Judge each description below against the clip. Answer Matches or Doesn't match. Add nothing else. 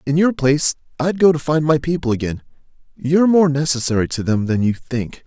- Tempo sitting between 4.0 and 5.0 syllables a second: Doesn't match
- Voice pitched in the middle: Matches